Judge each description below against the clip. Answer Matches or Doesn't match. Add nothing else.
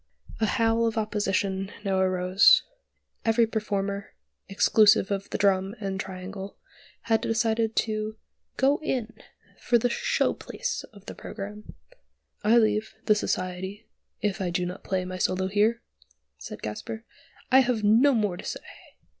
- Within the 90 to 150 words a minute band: Matches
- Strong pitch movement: Doesn't match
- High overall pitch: Matches